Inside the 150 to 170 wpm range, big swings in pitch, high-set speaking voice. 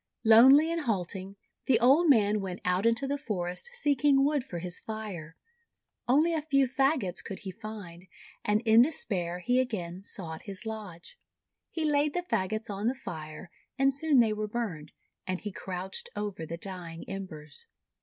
Yes: average, 165 wpm; wide, 6.7 semitones; high, 215 Hz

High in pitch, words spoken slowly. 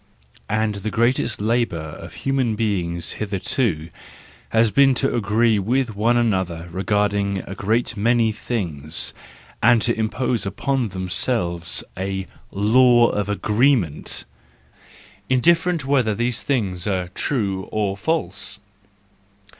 No: low, 110 Hz; slow, 115 wpm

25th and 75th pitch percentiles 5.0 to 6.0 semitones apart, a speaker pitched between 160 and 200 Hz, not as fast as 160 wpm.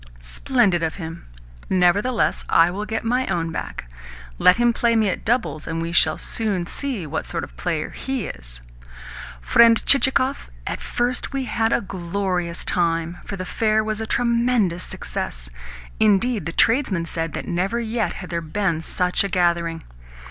No: wide, 5.4 semitones; high, 190 Hz; average, 170 wpm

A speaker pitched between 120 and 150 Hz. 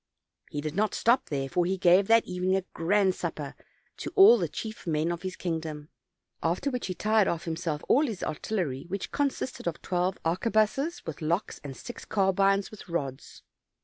No: medium, 180 Hz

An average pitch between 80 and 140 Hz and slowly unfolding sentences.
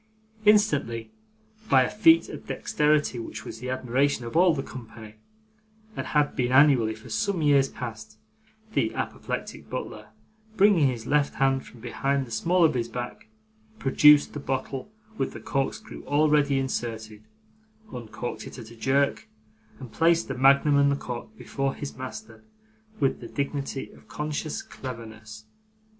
No: low, 135 Hz; average, 150 wpm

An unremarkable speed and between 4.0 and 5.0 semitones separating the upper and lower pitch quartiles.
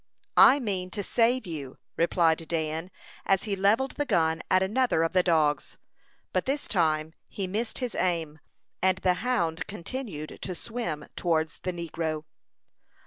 Yes: average, 150 wpm; average, 4.5 semitones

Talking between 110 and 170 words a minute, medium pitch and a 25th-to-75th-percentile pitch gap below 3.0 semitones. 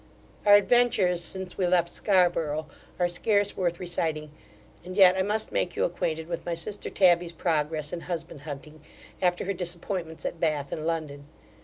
Yes: average, 165 wpm; medium, 175 Hz; narrow, 2.4 semitones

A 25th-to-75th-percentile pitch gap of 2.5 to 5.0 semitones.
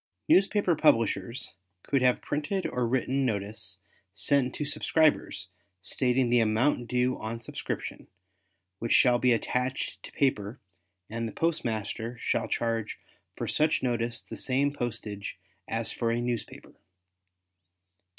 Yes: average, 3.1 semitones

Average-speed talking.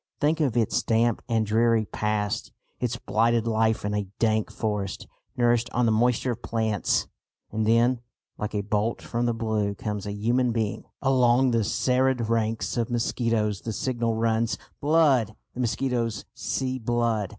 Yes: average, 160 wpm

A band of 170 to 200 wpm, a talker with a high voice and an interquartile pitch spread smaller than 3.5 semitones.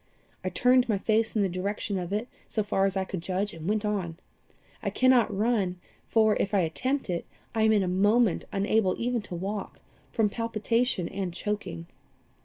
Yes: average, 190 wpm; high, 205 Hz; average, 3.0 semitones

